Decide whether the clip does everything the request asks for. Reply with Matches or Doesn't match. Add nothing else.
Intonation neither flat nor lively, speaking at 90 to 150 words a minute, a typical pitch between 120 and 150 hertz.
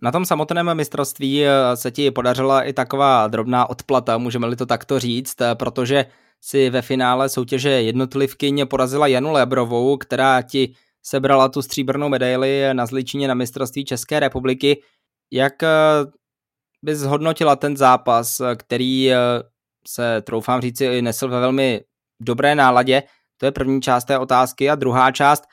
Doesn't match